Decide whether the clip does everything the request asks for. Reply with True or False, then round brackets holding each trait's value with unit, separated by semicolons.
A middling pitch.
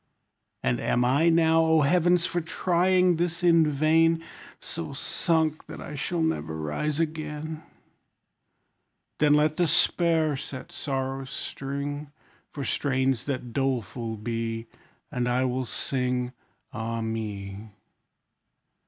True (145 Hz)